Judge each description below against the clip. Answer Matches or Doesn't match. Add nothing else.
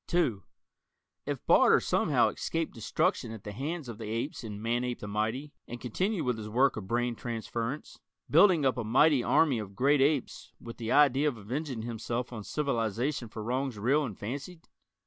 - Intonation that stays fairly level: Doesn't match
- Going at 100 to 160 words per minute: Doesn't match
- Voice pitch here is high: Doesn't match